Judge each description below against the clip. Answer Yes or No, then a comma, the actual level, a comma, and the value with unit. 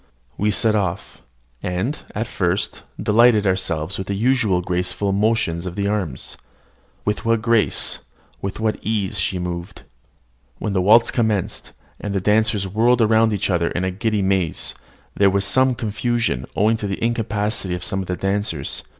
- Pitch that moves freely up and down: No, average, 3.0 semitones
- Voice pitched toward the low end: Yes, low, 100 Hz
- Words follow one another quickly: No, average, 165 wpm